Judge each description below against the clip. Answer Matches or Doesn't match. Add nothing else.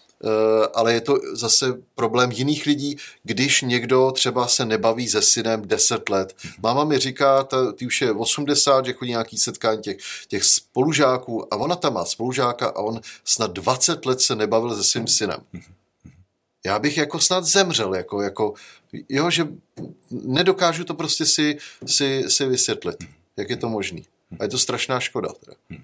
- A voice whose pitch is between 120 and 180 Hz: Matches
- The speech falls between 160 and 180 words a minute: Matches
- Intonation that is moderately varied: Matches